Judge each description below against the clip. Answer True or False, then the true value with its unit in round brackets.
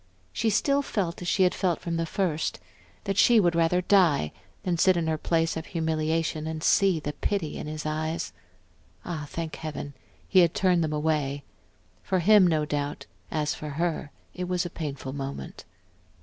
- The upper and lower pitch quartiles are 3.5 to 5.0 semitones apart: False (2.8 semitones)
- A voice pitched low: False (165 Hz)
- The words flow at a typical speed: True (180 wpm)